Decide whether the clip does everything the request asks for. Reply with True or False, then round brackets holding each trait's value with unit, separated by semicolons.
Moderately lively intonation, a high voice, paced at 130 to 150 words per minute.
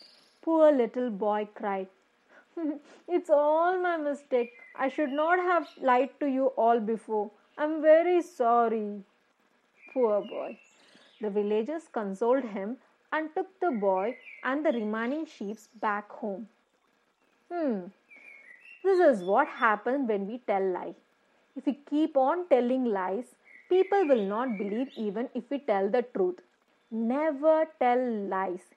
False (6.3 semitones; 250 Hz; 135 wpm)